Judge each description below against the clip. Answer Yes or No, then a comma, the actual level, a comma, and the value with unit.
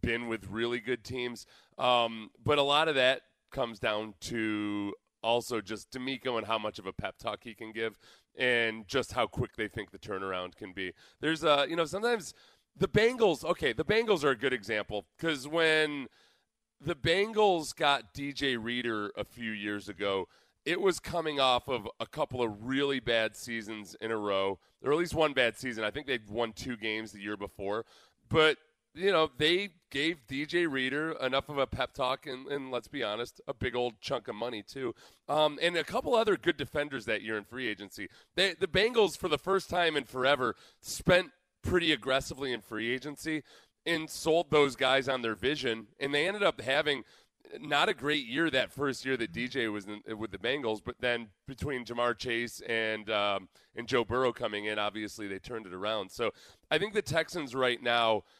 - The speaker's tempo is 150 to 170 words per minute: No, average, 200 wpm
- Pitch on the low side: Yes, low, 125 Hz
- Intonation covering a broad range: Yes, wide, 5.7 semitones